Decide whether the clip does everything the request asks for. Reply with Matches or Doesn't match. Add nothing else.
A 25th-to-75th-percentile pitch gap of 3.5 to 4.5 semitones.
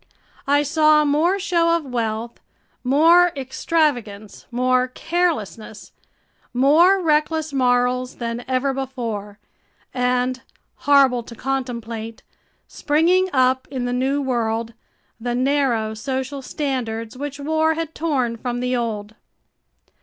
Matches